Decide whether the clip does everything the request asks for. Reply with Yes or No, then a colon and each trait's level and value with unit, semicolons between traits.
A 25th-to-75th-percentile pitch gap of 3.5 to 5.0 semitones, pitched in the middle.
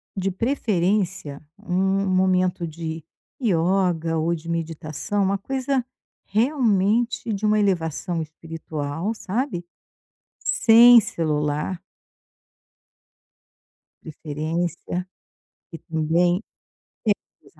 Yes: average, 4.1 semitones; medium, 180 Hz